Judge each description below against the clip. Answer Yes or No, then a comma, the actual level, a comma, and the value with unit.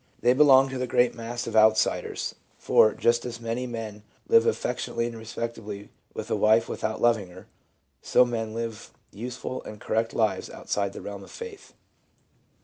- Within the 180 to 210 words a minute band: No, average, 170 wpm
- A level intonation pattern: Yes, narrow, 2.3 semitones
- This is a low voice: Yes, low, 115 Hz